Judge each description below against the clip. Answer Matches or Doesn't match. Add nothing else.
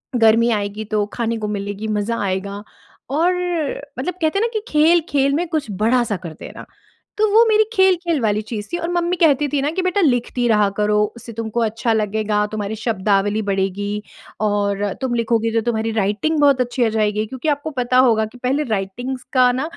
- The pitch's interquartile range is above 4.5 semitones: Matches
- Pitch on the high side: Matches